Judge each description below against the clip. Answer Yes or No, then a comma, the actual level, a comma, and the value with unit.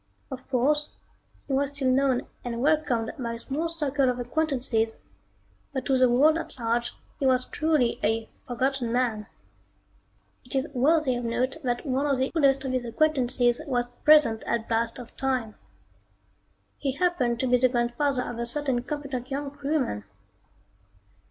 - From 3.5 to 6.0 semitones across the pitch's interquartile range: No, average, 2.8 semitones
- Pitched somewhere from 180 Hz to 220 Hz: No, very high, 255 Hz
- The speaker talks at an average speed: Yes, average, 160 wpm